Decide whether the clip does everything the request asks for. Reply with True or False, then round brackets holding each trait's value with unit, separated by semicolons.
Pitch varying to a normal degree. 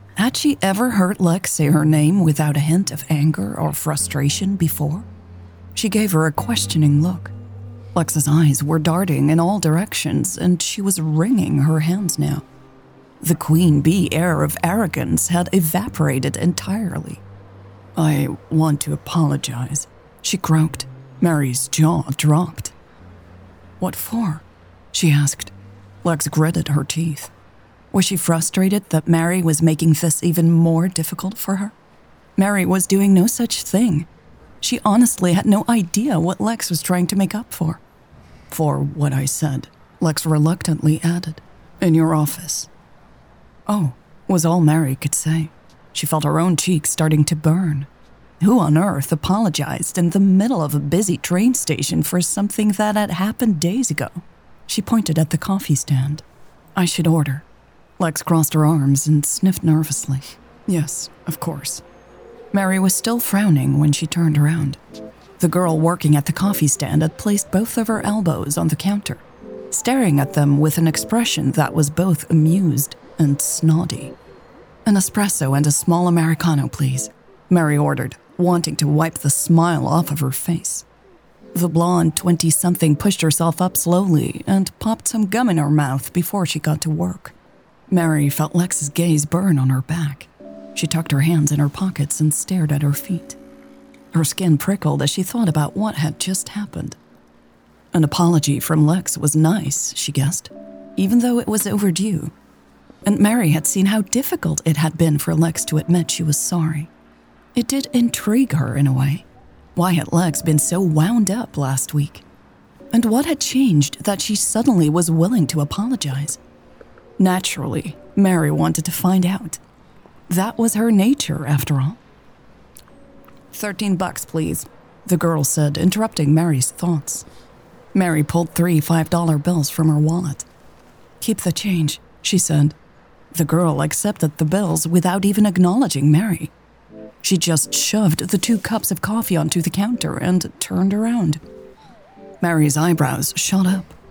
True (4.0 semitones)